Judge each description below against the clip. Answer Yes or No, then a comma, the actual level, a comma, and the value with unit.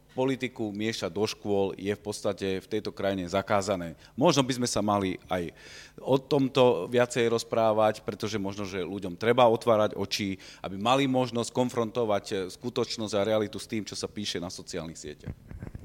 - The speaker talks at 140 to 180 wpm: Yes, fast, 165 wpm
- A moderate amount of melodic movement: Yes, average, 3.4 semitones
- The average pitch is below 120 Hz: Yes, low, 110 Hz